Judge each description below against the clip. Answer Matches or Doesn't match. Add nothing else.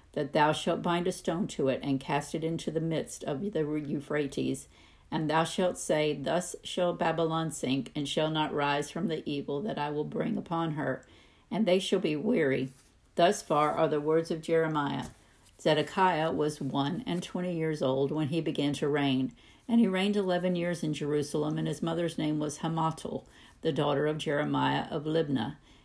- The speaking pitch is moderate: Matches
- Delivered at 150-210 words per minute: Matches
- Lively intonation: Doesn't match